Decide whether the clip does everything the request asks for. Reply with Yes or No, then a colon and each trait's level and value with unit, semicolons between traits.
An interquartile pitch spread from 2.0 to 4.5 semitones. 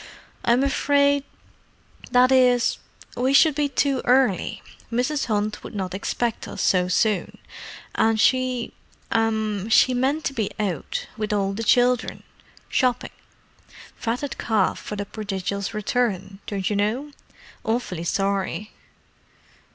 Yes: average, 4.1 semitones